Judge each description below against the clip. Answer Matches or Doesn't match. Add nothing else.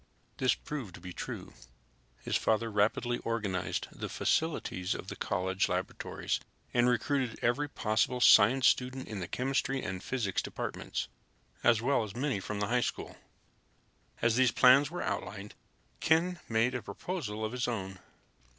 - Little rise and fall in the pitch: Doesn't match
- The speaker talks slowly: Doesn't match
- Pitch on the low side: Matches